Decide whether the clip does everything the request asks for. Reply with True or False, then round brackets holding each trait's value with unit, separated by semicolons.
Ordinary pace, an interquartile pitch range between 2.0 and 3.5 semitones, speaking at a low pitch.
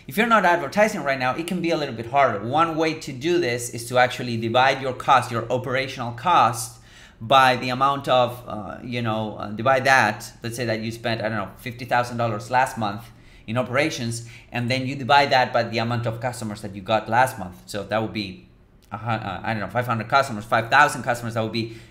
False (230 wpm; 2.8 semitones; 120 Hz)